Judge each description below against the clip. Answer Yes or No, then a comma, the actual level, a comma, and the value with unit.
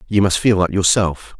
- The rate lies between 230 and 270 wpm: No, fast, 215 wpm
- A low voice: Yes, very low, 95 Hz